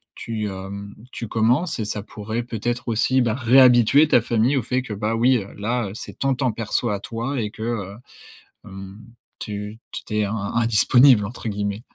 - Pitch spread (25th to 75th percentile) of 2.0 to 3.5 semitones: Yes, average, 2.9 semitones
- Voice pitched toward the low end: Yes, low, 115 Hz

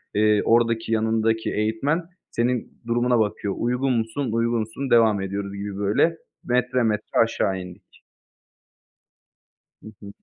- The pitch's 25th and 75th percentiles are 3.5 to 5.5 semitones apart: No, narrow, 2.4 semitones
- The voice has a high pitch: No, low, 110 Hz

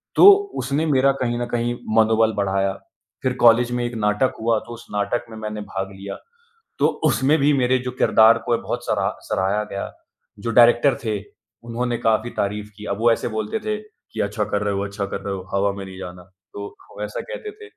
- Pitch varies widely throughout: No, average, 3.2 semitones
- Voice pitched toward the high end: No, low, 110 Hz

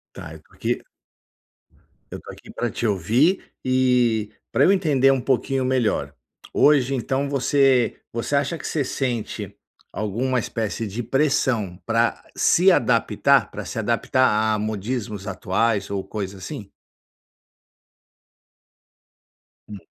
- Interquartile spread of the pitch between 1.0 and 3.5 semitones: No, average, 4.2 semitones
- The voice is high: No, low, 120 Hz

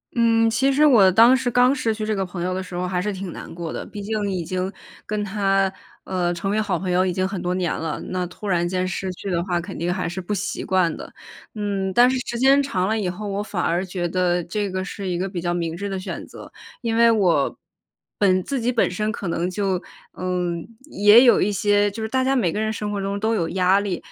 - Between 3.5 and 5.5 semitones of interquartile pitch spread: No, average, 3.0 semitones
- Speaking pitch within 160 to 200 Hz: Yes, high, 195 Hz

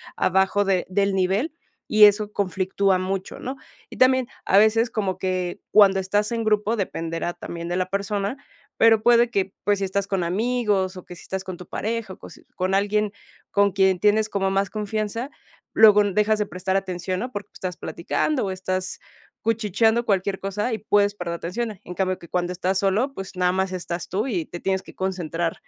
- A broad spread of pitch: No, narrow, 2.4 semitones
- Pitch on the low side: No, high, 195 Hz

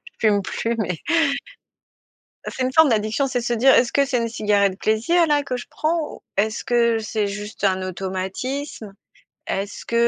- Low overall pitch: No, high, 225 Hz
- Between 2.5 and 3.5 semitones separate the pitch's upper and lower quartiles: No, average, 4.1 semitones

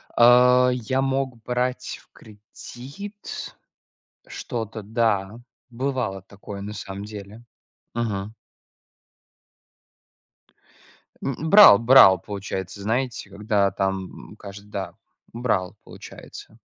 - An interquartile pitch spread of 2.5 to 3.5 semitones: No, average, 4.1 semitones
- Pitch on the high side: No, low, 110 Hz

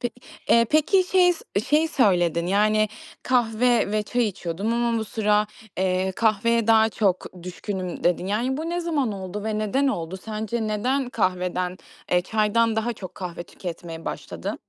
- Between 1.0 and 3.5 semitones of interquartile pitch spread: No, average, 4.2 semitones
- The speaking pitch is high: Yes, high, 215 Hz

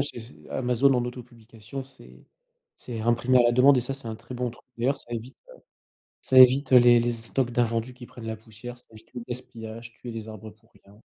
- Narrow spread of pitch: Yes, narrow, 1.9 semitones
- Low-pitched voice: Yes, low, 120 Hz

